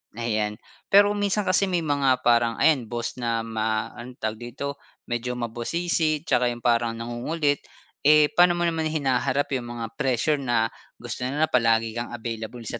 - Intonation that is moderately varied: Yes, average, 4.5 semitones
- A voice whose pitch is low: Yes, low, 120 Hz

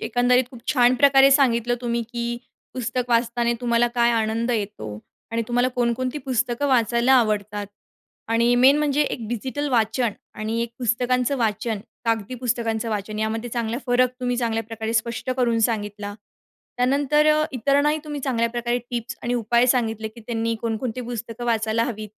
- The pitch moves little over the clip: Yes, narrow, 1.9 semitones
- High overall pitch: Yes, high, 235 Hz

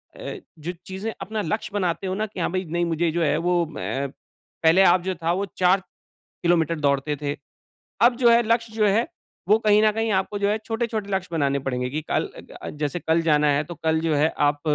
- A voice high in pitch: No, medium, 175 Hz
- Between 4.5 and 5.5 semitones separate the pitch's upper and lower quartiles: Yes, average, 5.0 semitones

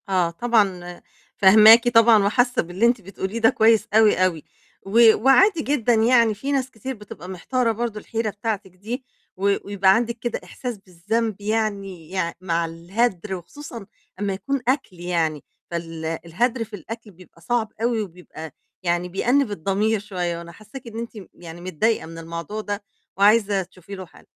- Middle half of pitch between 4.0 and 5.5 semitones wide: Yes, average, 4.3 semitones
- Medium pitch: No, high, 205 Hz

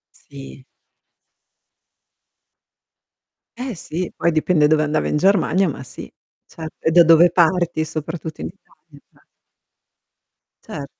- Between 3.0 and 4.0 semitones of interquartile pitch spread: No, narrow, 2.4 semitones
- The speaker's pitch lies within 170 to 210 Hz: No, medium, 160 Hz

